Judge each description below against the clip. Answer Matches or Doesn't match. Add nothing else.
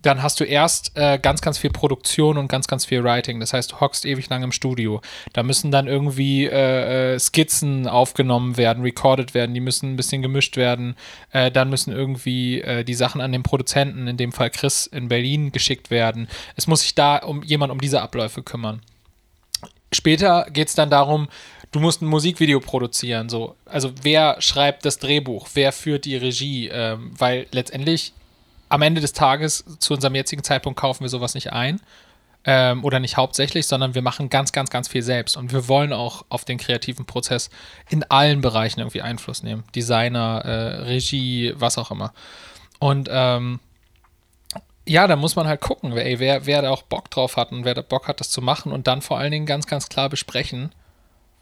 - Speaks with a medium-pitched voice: Doesn't match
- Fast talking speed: Matches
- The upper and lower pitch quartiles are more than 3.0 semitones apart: Doesn't match